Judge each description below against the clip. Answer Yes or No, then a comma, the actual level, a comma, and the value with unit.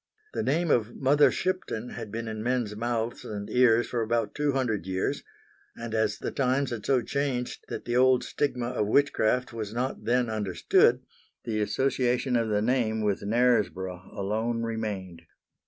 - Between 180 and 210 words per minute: No, average, 165 wpm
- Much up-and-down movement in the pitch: No, average, 2.8 semitones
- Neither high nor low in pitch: No, low, 115 Hz